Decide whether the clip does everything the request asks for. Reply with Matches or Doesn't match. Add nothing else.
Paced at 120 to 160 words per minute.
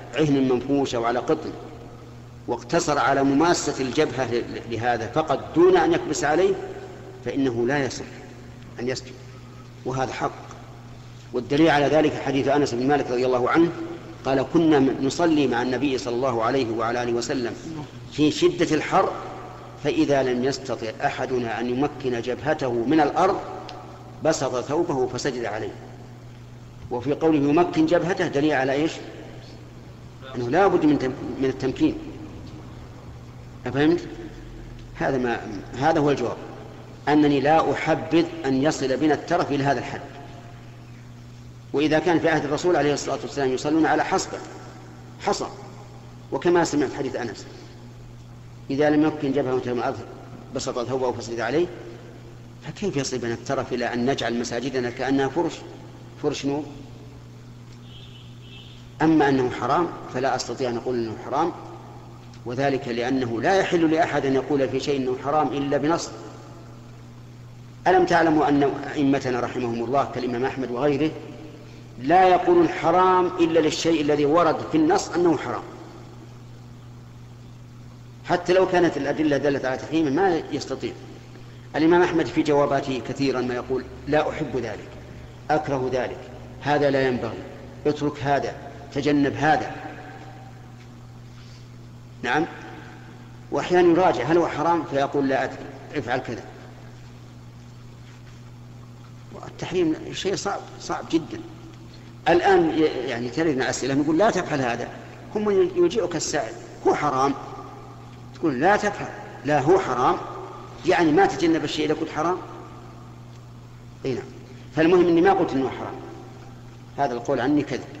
Matches